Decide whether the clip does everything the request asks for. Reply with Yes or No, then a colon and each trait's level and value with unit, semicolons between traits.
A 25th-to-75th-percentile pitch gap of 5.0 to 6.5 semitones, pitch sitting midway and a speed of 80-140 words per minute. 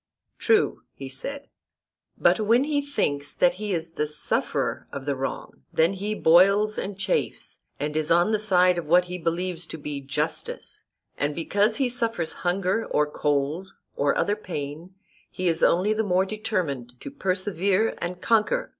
No: average, 5.3 semitones; medium, 180 Hz; average, 165 wpm